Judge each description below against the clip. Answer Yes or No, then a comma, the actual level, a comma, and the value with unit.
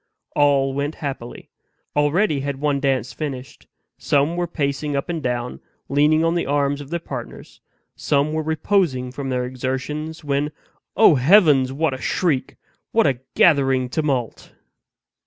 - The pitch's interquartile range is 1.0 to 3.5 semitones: Yes, average, 2.9 semitones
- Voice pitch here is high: No, medium, 140 Hz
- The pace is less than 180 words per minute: Yes, average, 145 wpm